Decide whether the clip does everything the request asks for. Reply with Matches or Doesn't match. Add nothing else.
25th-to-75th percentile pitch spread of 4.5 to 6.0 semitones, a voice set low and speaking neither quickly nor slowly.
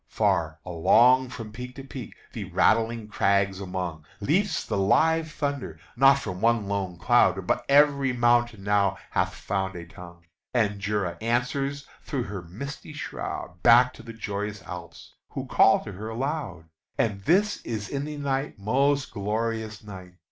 Matches